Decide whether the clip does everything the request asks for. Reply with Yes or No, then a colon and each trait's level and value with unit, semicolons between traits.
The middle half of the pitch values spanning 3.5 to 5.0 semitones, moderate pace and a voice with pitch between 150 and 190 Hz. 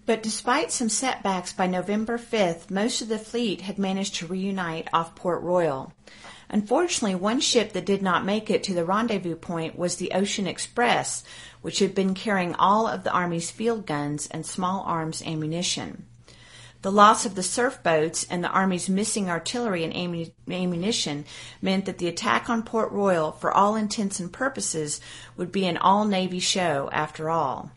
Yes: average, 4.0 semitones; average, 175 wpm; medium, 185 Hz